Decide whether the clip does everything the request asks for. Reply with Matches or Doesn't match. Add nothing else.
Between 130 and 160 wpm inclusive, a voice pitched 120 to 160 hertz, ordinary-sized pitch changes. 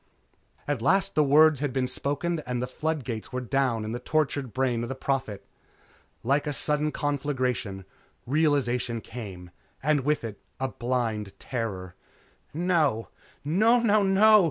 Matches